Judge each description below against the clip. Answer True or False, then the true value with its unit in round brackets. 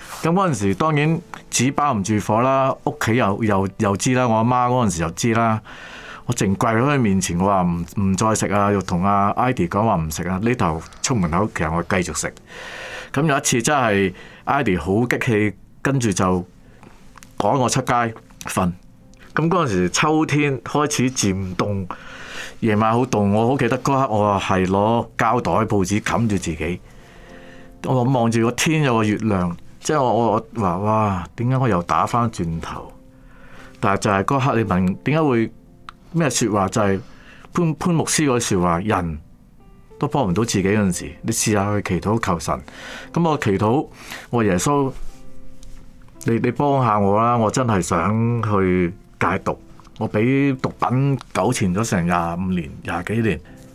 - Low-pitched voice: True (105 Hz)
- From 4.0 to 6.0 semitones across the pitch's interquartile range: True (4.9 semitones)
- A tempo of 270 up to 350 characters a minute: False (240 characters per minute)